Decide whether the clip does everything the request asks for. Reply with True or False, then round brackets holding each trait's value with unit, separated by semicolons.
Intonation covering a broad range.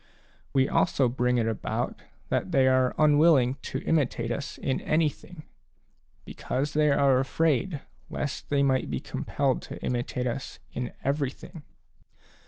False (2.9 semitones)